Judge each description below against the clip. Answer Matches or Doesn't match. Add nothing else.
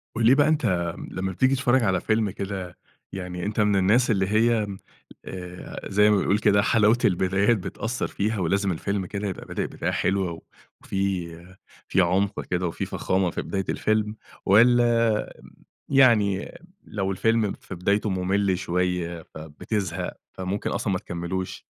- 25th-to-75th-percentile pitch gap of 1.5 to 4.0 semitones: Matches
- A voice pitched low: Matches